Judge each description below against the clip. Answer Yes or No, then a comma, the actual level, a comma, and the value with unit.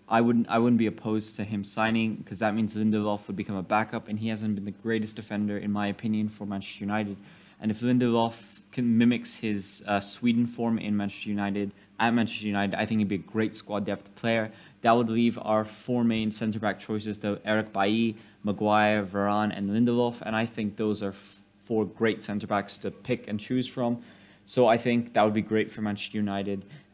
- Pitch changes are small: Yes, narrow, 1.8 semitones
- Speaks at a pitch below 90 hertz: No, low, 105 Hz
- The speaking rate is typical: No, fast, 210 wpm